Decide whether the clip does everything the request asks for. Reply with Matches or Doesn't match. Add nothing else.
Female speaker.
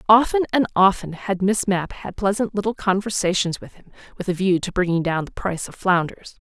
Matches